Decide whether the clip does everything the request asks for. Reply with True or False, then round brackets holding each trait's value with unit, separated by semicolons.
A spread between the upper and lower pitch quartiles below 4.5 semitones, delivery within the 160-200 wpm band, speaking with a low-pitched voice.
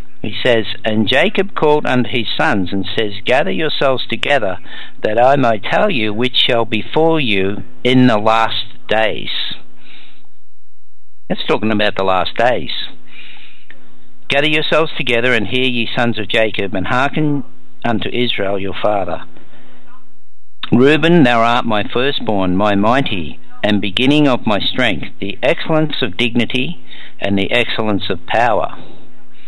False (3.7 semitones; 140 wpm; 120 Hz)